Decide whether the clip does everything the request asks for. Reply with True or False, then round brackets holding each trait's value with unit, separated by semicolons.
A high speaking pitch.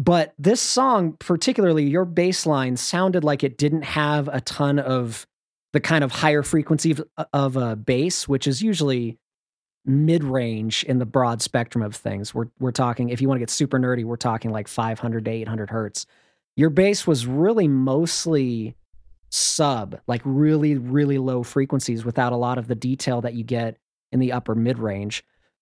False (130 Hz)